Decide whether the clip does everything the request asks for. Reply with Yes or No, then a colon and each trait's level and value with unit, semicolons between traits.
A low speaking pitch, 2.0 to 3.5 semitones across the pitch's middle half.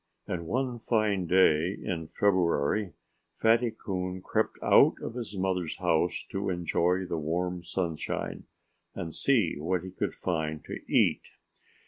Yes: very low, 90 Hz; average, 3.2 semitones